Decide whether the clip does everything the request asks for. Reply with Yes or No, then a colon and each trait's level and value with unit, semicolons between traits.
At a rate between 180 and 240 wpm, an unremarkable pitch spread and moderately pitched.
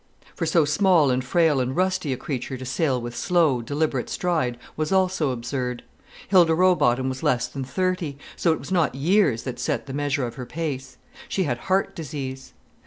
Yes: average, 185 wpm; average, 5.0 semitones; medium, 145 Hz